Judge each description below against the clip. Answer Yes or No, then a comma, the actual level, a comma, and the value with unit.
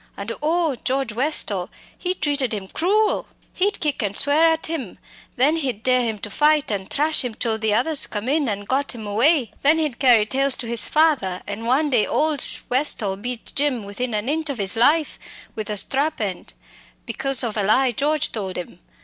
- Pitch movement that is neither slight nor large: No, wide, 5.8 semitones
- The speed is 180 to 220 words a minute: Yes, average, 200 wpm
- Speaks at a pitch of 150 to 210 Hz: No, very high, 255 Hz